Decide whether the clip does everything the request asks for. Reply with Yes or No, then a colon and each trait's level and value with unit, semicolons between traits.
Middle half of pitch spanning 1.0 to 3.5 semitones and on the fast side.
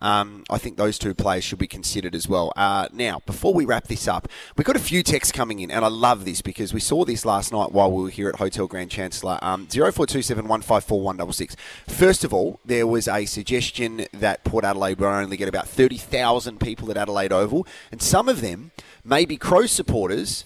Yes: average, 2.8 semitones; fast, 220 wpm